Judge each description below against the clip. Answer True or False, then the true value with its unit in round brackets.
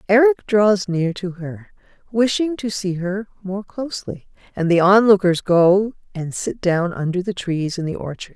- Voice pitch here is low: False (195 Hz)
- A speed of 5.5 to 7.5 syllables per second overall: False (4.6 syllables/s)